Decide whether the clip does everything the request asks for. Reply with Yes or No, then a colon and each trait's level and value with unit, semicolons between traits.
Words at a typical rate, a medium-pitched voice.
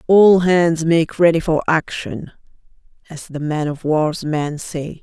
Yes: average, 155 wpm; medium, 160 Hz